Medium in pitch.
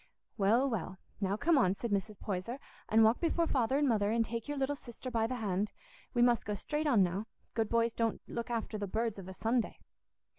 No: high, 225 Hz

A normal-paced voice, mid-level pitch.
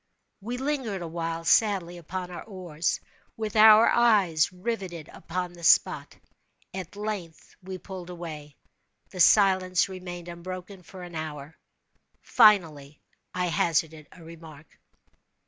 No: slow, 120 wpm; medium, 180 Hz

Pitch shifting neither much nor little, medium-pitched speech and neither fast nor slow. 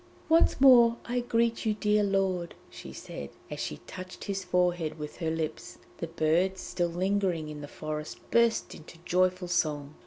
Yes: average, 4.4 semitones; medium, 180 Hz; average, 175 wpm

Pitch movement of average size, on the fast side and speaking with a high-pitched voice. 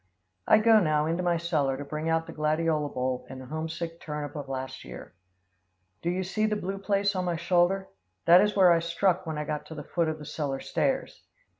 No: average, 3.3 semitones; fast, 220 wpm; medium, 165 Hz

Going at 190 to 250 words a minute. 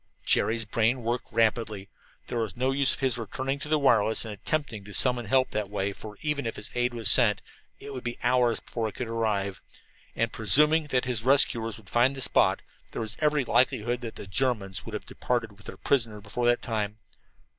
Yes: fast, 205 wpm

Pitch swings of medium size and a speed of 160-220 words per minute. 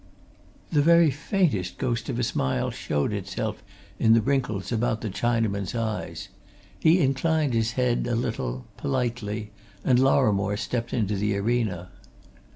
No: average, 3.7 semitones; average, 140 wpm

